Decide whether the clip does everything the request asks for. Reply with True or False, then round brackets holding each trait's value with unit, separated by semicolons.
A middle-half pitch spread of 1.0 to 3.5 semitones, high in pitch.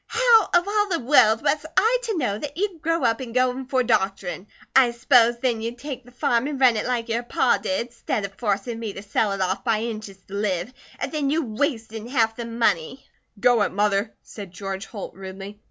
False (4.4 semitones; 235 Hz)